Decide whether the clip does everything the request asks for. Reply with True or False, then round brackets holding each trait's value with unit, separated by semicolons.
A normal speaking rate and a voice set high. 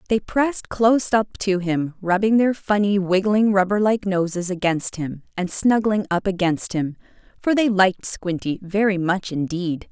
True (165 wpm; 195 Hz)